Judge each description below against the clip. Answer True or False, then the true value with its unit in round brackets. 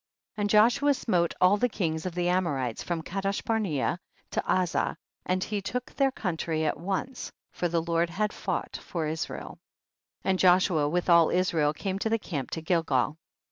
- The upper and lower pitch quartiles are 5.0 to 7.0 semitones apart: False (3.7 semitones)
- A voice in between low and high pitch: True (180 Hz)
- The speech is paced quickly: False (185 wpm)